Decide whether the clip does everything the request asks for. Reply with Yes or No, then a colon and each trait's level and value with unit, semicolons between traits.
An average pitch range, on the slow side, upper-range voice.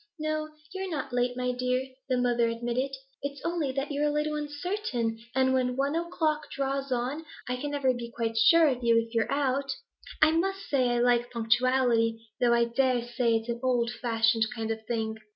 No: average, 3.4 semitones; average, 195 wpm; very high, 250 Hz